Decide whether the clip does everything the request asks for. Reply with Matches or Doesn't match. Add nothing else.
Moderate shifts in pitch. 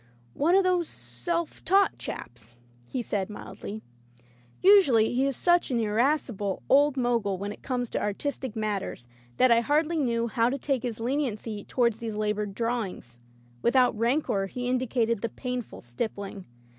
Matches